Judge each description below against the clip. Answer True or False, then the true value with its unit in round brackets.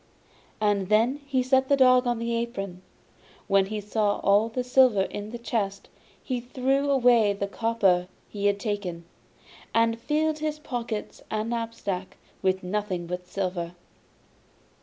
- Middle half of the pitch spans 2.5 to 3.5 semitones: False (4.0 semitones)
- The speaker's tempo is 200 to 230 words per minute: False (145 wpm)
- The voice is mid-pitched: False (220 Hz)